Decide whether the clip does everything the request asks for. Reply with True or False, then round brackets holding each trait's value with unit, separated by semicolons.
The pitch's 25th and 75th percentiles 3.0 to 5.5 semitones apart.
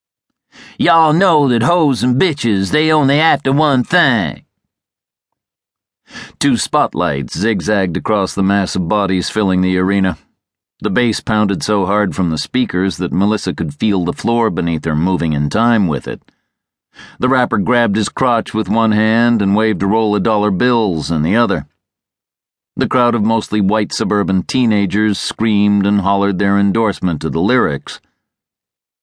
True (3.8 semitones)